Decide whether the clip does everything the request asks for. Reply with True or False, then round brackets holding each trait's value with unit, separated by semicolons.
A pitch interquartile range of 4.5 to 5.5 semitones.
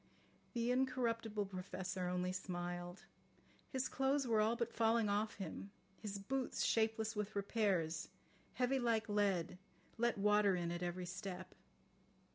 False (4.0 semitones)